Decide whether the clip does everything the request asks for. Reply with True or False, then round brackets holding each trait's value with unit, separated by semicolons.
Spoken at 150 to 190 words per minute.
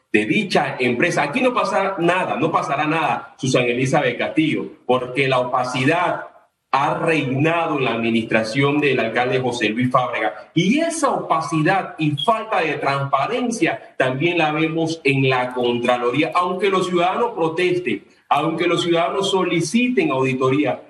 False (140 wpm)